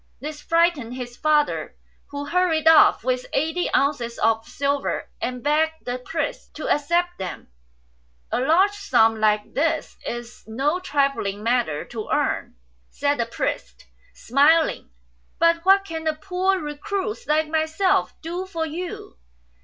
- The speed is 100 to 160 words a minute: Yes, average, 145 wpm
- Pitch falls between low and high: No, very high, 295 Hz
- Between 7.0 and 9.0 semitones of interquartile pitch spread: No, average, 5.3 semitones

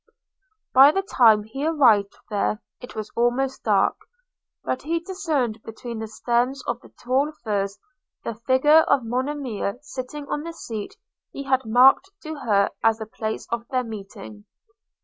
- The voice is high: Yes, high, 245 Hz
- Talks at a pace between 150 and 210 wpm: Yes, average, 155 wpm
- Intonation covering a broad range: No, average, 4.1 semitones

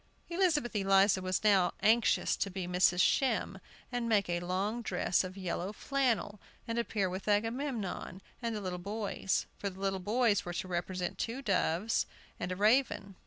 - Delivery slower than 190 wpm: Yes, average, 165 wpm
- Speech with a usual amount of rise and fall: Yes, average, 3.8 semitones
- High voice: Yes, high, 200 Hz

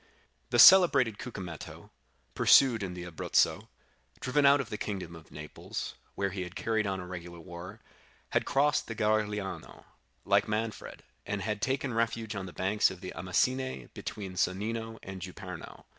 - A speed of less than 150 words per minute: No, average, 160 wpm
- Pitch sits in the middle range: No, low, 105 Hz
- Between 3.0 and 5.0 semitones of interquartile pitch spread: Yes, average, 3.8 semitones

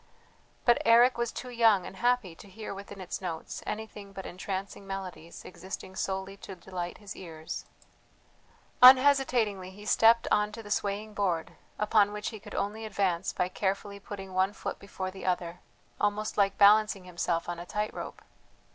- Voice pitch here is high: Yes, high, 200 Hz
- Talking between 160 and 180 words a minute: Yes, average, 165 wpm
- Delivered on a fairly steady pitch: Yes, narrow, 2.3 semitones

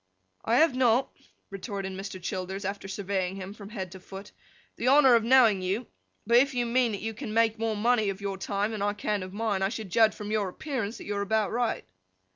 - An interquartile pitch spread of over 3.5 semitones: No, average, 3.0 semitones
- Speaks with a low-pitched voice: No, high, 210 Hz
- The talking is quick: Yes, fast, 225 wpm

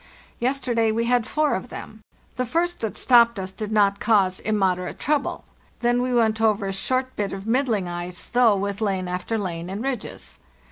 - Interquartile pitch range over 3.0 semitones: Yes, average, 4.1 semitones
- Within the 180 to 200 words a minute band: Yes, average, 185 wpm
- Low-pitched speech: No, high, 220 Hz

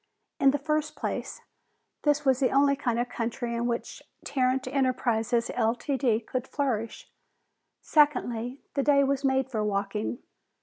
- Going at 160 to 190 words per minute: No, average, 140 wpm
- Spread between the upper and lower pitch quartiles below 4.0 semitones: Yes, average, 3.0 semitones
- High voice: Yes, very high, 255 Hz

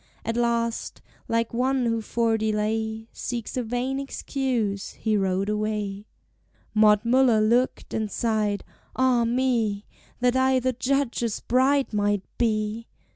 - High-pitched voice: Yes, high, 230 Hz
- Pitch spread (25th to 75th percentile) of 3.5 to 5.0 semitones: No, average, 2.8 semitones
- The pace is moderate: No, slow, 130 wpm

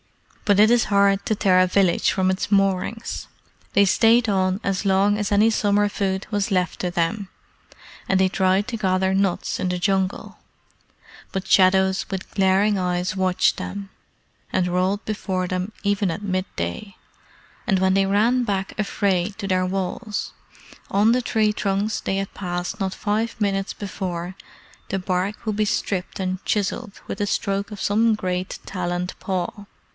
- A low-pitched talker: No, high, 195 Hz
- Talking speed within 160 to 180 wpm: Yes, average, 165 wpm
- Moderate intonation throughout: No, narrow, 1.8 semitones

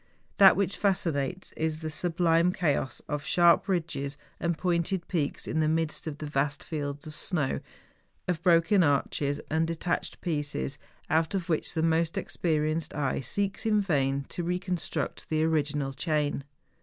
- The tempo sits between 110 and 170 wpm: Yes, average, 155 wpm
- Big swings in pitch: No, average, 3.1 semitones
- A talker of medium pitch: Yes, medium, 160 Hz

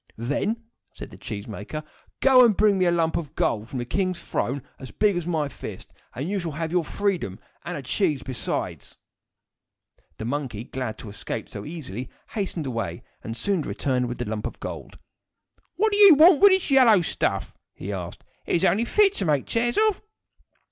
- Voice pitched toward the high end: No, medium, 165 Hz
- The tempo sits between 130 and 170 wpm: No, average, 195 wpm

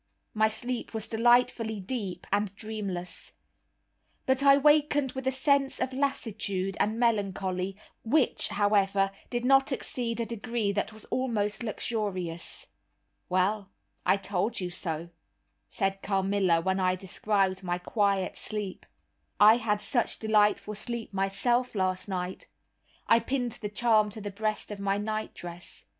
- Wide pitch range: No, average, 3.5 semitones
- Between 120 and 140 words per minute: Yes, slow, 135 wpm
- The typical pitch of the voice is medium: No, high, 210 Hz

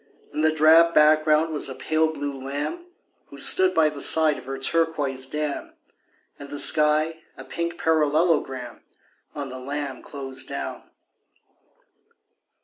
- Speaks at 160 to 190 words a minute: No, average, 140 wpm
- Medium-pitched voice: Yes, medium, 150 Hz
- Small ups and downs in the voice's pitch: Yes, narrow, 2.3 semitones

